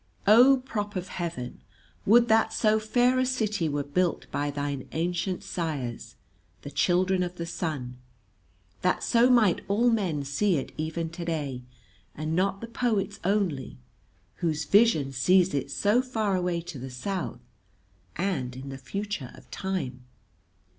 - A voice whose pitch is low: No, medium, 180 Hz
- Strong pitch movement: Yes, wide, 6.3 semitones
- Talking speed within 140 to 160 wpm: Yes, average, 145 wpm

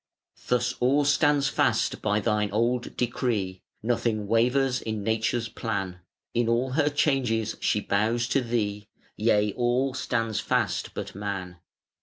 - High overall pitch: No, low, 115 Hz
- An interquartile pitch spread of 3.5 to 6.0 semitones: No, average, 3.0 semitones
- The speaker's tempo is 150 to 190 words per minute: No, slow, 135 wpm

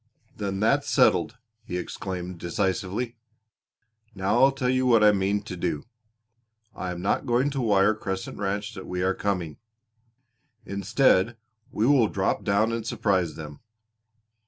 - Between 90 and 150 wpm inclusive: Yes, average, 145 wpm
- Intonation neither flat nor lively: Yes, average, 3.6 semitones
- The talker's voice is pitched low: Yes, low, 100 Hz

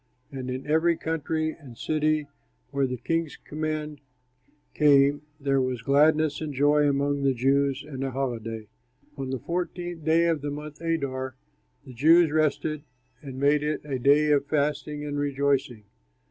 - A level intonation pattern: Yes, narrow, 2.2 semitones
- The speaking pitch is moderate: Yes, medium, 145 Hz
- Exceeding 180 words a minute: No, average, 155 wpm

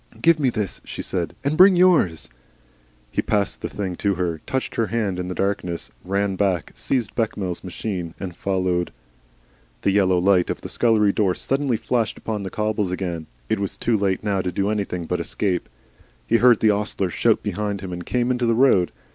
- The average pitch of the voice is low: Yes, low, 100 Hz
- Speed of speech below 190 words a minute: No, average, 195 wpm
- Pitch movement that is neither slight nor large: Yes, average, 3.7 semitones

